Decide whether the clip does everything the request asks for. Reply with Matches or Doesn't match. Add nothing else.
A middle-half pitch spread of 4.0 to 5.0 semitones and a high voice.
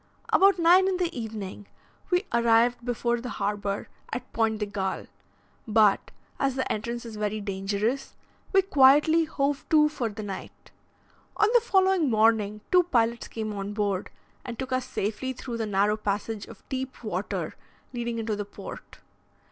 Matches